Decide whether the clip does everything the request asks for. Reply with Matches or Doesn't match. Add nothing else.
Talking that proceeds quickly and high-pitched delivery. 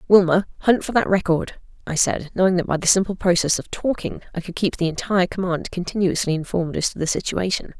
Doesn't match